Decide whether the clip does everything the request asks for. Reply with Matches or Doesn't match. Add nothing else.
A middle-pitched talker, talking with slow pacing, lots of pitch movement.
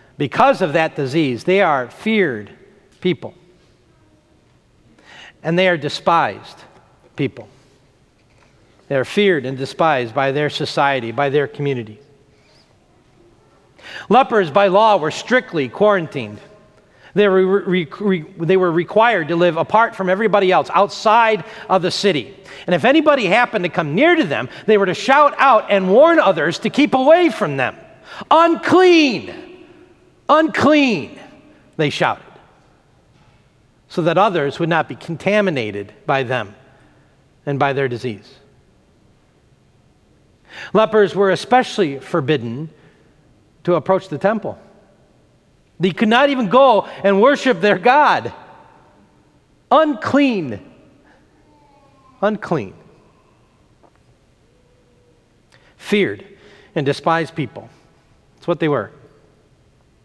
Matches